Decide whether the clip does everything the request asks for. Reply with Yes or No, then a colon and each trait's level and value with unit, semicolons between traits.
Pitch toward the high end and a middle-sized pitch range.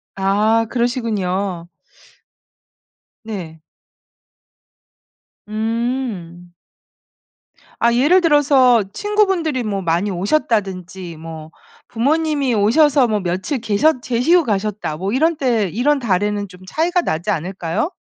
No: high, 220 Hz; wide, 6.2 semitones